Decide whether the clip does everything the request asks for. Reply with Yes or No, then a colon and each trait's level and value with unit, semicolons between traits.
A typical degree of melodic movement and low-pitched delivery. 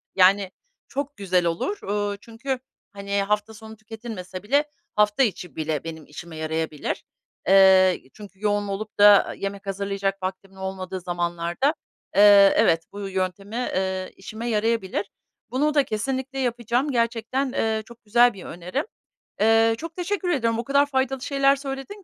No: average, 4.5 semitones; high, 210 Hz